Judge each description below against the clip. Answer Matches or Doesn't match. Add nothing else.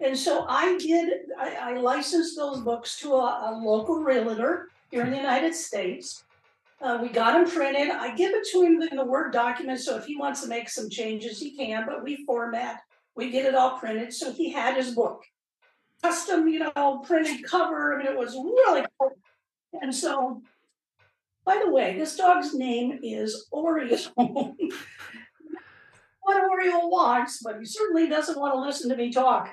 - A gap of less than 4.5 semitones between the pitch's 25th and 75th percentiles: Doesn't match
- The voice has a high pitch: Matches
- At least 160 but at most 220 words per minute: Matches